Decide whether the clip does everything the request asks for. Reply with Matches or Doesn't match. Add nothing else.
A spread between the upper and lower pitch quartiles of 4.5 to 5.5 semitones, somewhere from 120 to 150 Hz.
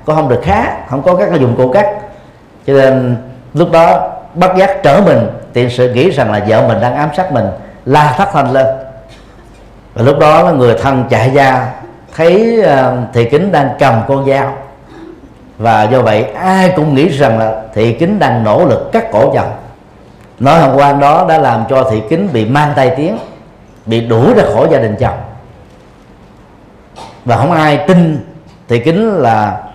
Matches